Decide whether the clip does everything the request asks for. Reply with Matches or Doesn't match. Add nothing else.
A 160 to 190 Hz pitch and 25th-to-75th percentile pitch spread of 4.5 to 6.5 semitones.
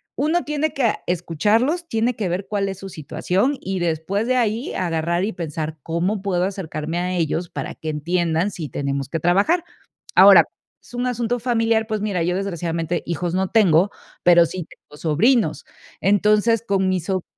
Matches